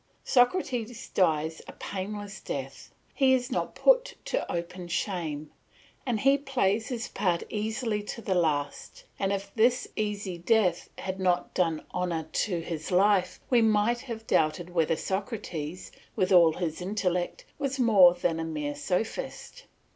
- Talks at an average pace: Yes, average, 145 wpm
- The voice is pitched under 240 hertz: Yes, high, 190 Hz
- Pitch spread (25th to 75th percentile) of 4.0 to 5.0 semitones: Yes, average, 4.7 semitones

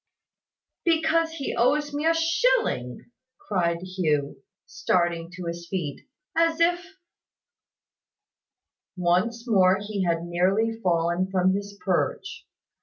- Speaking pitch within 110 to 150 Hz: No, high, 190 Hz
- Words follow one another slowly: Yes, slow, 110 wpm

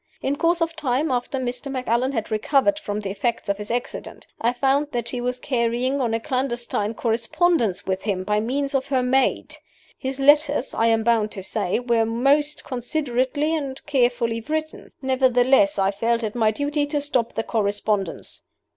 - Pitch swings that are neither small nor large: Yes, average, 3.7 semitones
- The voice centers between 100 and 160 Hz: No, high, 245 Hz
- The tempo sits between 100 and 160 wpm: No, average, 175 wpm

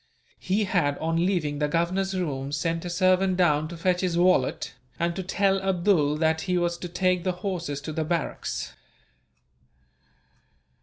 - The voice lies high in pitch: No, medium, 175 Hz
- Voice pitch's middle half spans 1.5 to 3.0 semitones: Yes, average, 2.7 semitones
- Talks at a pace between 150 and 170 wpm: Yes, average, 160 wpm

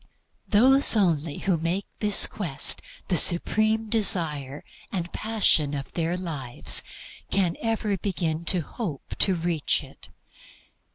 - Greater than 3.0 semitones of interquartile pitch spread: Yes, average, 4.7 semitones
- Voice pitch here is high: No, medium, 175 Hz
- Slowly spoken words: Yes, slow, 120 wpm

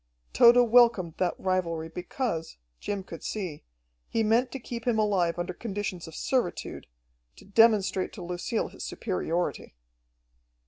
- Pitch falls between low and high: No, high, 195 Hz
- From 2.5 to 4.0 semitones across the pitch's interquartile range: No, average, 4.5 semitones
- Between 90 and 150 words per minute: Yes, slow, 135 wpm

